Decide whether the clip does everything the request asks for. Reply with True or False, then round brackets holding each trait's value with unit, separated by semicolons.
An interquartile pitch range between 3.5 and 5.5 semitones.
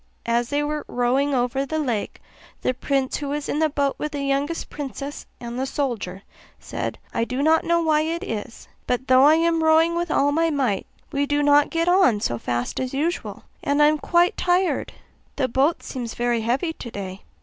True (4.2 semitones)